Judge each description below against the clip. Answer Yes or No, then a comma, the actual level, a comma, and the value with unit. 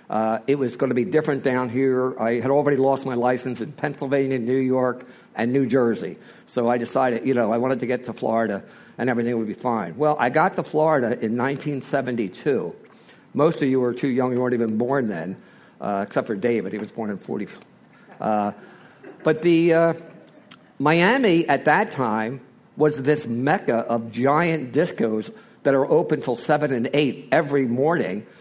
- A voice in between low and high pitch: No, low, 130 Hz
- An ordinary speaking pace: Yes, average, 190 wpm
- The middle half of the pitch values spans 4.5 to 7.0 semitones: No, average, 3.7 semitones